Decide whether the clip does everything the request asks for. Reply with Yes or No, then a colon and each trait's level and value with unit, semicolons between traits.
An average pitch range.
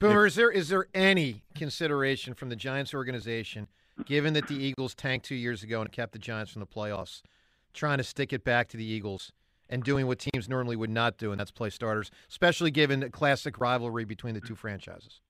Yes: average, 4.2 semitones